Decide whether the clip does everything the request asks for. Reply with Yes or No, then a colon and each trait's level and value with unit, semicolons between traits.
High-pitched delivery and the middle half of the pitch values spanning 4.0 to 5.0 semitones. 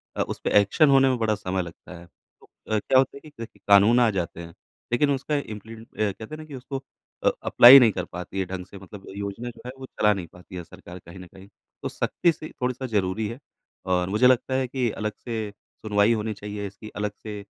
No: low, 105 Hz; average, 4.6 semitones